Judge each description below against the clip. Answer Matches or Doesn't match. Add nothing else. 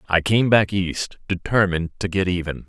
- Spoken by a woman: Doesn't match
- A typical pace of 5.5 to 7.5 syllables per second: Doesn't match